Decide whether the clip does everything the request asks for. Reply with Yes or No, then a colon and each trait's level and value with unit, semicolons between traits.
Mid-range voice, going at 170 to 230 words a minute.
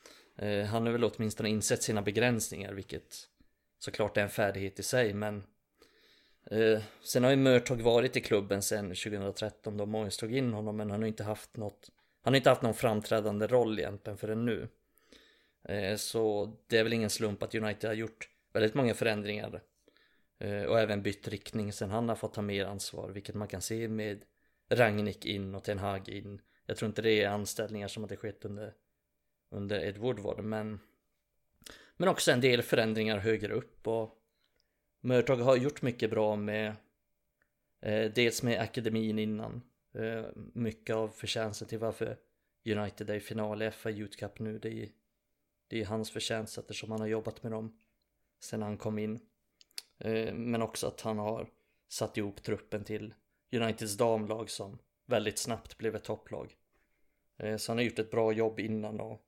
No: low, 110 Hz; average, 175 wpm